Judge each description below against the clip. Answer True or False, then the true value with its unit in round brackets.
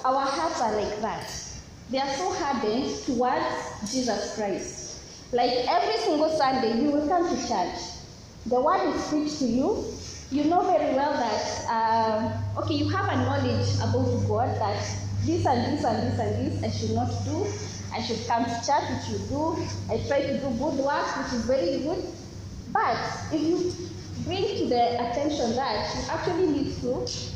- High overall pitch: True (245 Hz)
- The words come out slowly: False (180 wpm)